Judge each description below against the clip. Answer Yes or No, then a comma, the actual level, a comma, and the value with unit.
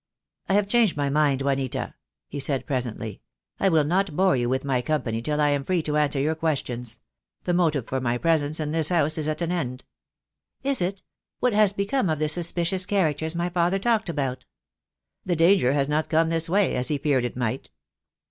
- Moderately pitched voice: Yes, medium, 155 Hz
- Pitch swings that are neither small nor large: Yes, average, 4.4 semitones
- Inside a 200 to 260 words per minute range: Yes, fast, 205 wpm